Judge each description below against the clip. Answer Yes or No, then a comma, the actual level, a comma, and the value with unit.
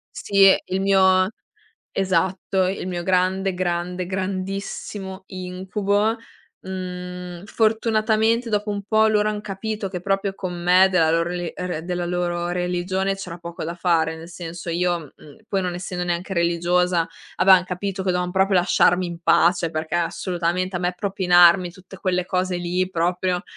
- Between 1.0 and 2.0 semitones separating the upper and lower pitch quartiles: Yes, narrow, 1.6 semitones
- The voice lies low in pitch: No, medium, 185 Hz